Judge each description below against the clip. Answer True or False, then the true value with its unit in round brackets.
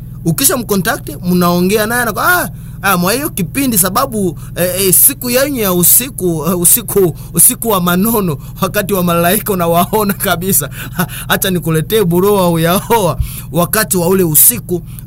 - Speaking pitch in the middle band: True (180 Hz)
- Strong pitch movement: False (3.9 semitones)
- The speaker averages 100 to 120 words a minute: False (135 wpm)